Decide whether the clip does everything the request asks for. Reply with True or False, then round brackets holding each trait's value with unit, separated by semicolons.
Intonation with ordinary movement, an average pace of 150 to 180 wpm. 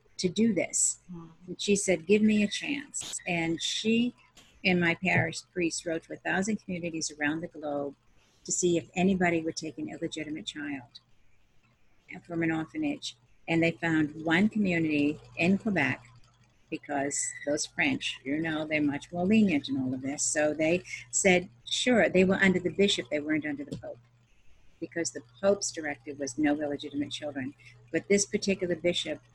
True (4.0 semitones; 170 wpm)